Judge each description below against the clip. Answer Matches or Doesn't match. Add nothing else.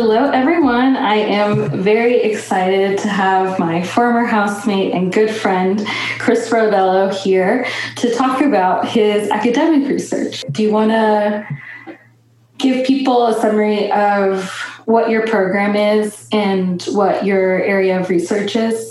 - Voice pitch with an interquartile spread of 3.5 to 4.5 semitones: Doesn't match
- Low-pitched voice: Doesn't match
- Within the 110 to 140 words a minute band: Matches